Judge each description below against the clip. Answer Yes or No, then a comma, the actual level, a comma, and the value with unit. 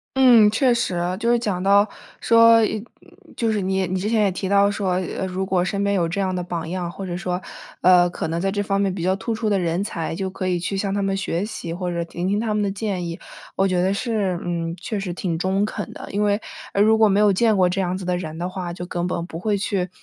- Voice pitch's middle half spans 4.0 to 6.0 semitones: No, narrow, 2.4 semitones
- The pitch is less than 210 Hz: Yes, high, 190 Hz